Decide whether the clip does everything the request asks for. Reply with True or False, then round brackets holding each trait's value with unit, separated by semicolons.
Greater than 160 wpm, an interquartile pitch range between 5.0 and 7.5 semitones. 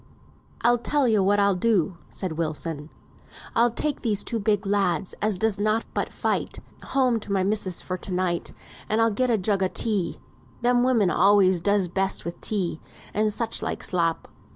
False (180 wpm; 3.5 semitones)